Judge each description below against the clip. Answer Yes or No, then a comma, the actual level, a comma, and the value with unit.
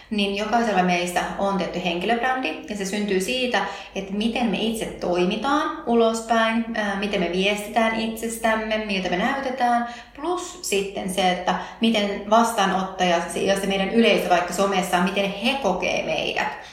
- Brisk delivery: No, average, 145 wpm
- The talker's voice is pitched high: Yes, high, 205 Hz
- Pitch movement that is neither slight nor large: Yes, average, 3.3 semitones